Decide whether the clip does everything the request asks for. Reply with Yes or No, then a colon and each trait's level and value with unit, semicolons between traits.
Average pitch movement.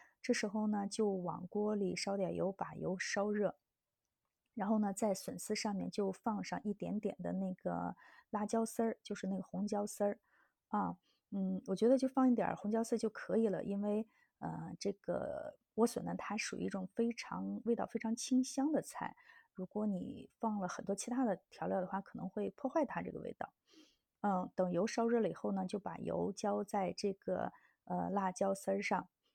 Yes: average, 3.0 semitones